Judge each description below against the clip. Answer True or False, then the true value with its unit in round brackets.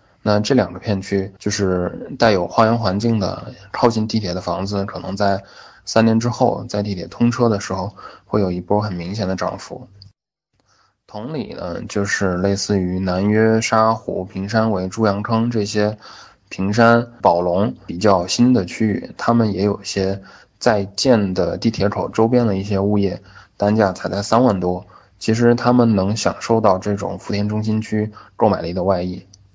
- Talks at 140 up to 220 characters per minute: False (250 characters per minute)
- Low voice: True (105 Hz)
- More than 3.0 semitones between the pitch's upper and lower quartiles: False (2.6 semitones)